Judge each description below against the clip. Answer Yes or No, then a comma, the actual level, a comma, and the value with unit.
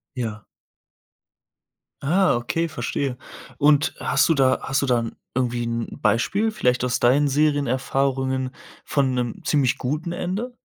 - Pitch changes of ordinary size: Yes, average, 3.3 semitones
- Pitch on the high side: No, low, 135 Hz